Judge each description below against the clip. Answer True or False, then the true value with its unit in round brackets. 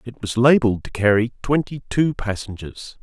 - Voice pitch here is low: True (115 Hz)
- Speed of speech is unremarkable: True (160 wpm)